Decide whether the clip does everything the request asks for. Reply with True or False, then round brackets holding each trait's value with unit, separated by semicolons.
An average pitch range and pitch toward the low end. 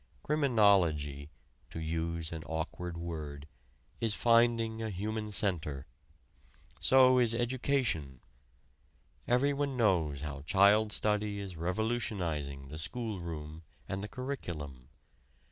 False (6.6 semitones; 95 Hz)